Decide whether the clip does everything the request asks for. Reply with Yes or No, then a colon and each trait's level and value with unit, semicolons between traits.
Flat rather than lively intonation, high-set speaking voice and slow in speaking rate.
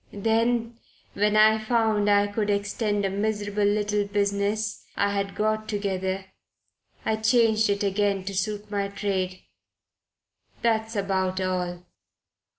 Yes: narrow, 1.5 semitones; high, 205 Hz; slow, 125 wpm